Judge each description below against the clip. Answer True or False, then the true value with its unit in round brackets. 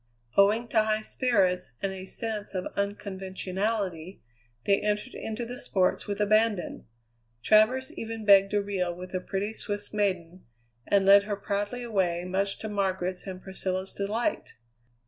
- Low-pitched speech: False (200 Hz)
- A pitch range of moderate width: False (2.2 semitones)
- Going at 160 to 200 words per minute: False (145 wpm)